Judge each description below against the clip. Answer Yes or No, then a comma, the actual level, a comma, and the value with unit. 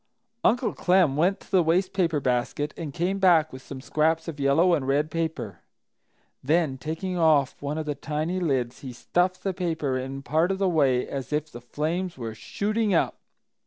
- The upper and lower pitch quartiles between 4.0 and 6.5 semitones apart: Yes, average, 4.4 semitones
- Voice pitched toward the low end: No, medium, 155 Hz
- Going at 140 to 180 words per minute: No, average, 190 wpm